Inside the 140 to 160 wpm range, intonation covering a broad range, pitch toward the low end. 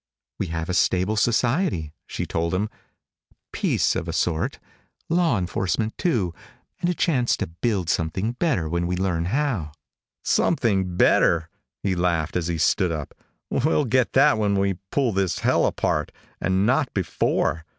Yes: average, 155 wpm; wide, 5.9 semitones; very low, 95 Hz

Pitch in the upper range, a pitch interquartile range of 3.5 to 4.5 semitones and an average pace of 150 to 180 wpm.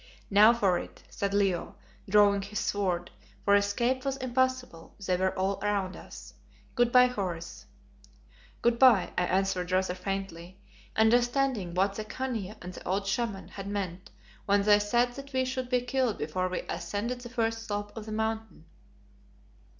Yes: high, 205 Hz; average, 4.2 semitones; average, 160 wpm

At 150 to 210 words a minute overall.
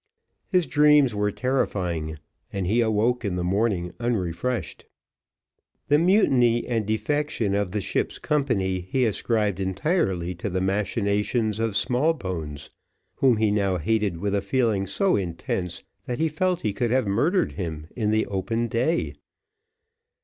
No: average, 140 wpm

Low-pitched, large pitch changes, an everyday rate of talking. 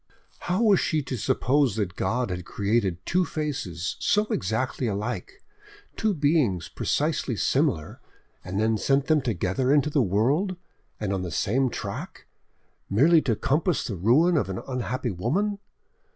Yes: low, 125 Hz; wide, 7.5 semitones; average, 150 wpm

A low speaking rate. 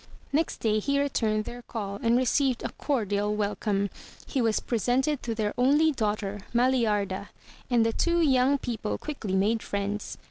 No: average, 165 wpm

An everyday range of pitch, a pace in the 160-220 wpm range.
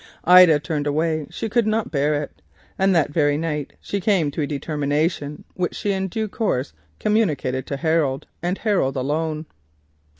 Yes: average, 4.5 semitones; average, 165 wpm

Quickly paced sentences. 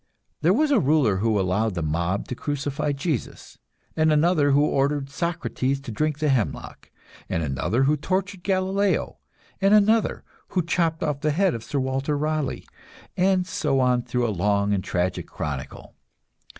No: average, 165 wpm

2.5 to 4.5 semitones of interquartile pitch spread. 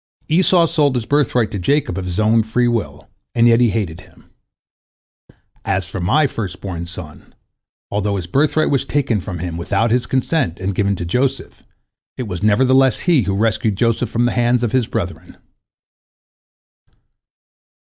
No: average, 5.1 semitones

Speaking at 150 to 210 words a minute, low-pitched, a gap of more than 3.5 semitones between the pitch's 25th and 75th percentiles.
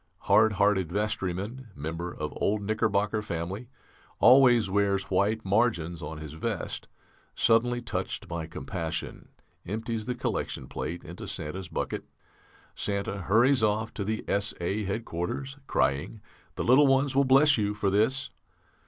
No: slow, 135 wpm; low, 105 Hz; average, 4.6 semitones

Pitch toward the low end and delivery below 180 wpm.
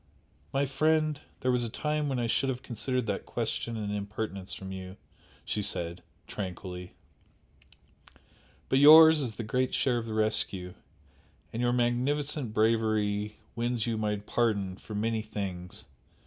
Yes: low, 115 Hz; average, 150 wpm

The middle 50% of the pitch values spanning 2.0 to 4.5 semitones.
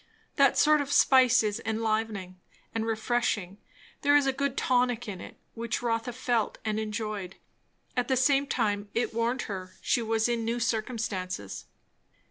Yes: average, 2.7 semitones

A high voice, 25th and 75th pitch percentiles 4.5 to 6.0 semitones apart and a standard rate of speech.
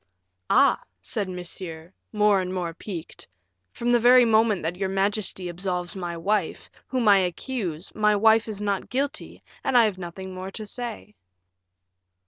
No: high, 195 Hz; average, 3.5 semitones; average, 155 wpm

